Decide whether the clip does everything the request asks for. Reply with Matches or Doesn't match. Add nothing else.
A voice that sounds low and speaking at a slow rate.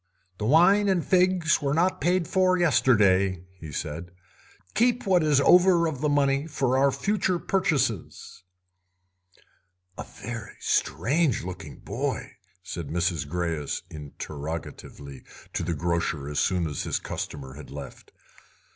Matches